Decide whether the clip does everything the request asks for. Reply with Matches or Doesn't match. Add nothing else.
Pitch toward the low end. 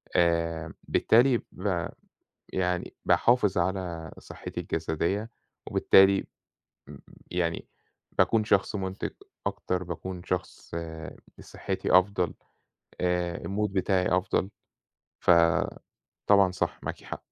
Matches